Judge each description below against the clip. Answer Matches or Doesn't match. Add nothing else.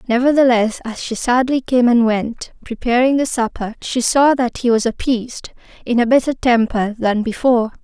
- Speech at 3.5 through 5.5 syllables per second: Matches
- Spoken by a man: Doesn't match